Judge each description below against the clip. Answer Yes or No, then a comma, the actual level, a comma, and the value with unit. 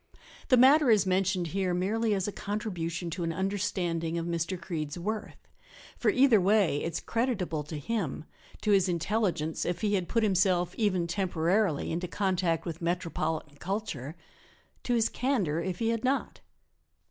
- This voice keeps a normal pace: Yes, average, 160 wpm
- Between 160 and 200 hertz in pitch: Yes, medium, 185 Hz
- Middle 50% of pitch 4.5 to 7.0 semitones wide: No, average, 4.0 semitones